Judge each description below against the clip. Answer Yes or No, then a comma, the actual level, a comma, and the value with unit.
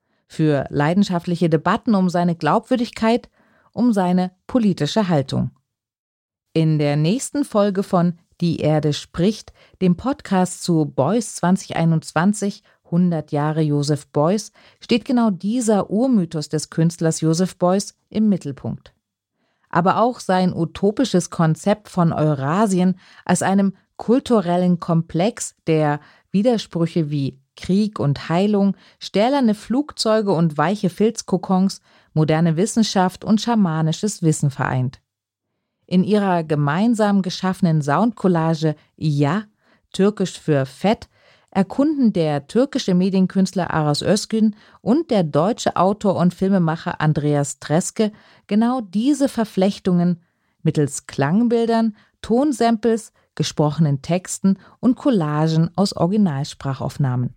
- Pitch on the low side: No, medium, 185 Hz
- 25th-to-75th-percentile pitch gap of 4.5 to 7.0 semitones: Yes, average, 5.0 semitones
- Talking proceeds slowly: Yes, slow, 105 wpm